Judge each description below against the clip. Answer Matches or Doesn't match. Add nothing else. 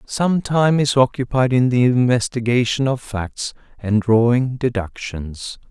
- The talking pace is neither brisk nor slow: Doesn't match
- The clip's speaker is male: Matches